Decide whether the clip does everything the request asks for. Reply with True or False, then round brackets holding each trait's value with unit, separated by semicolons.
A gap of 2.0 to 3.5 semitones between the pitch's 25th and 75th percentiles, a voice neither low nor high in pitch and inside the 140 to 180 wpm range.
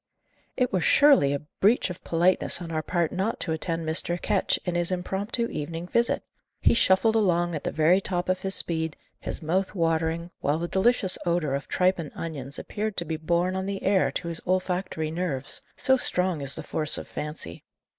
False (2.9 semitones; 175 Hz; 195 wpm)